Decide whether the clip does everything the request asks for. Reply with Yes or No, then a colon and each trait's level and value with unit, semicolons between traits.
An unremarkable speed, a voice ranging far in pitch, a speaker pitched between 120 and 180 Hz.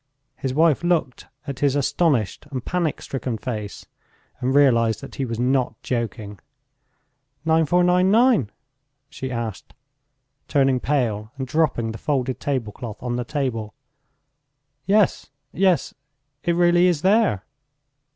No: slow, 120 wpm; wide, 5.7 semitones; low, 135 Hz